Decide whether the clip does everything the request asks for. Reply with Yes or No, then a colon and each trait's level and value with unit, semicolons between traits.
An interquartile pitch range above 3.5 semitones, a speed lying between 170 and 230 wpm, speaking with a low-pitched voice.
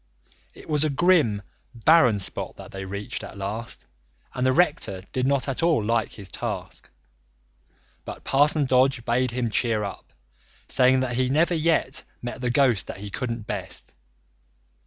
No: average, 4.5 semitones; average, 160 wpm; low, 125 Hz